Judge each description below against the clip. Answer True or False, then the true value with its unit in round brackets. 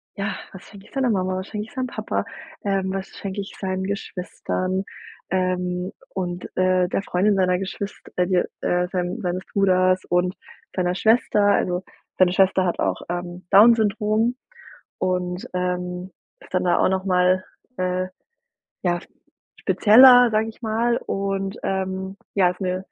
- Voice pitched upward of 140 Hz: True (190 Hz)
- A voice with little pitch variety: True (1.8 semitones)